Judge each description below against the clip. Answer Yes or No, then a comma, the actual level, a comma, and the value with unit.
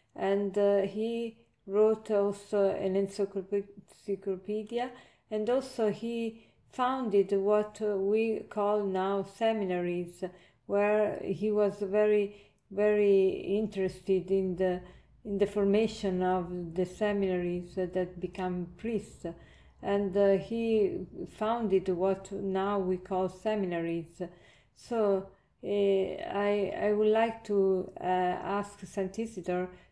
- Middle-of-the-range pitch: No, high, 200 Hz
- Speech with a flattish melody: Yes, narrow, 2.0 semitones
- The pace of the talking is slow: Yes, slow, 105 wpm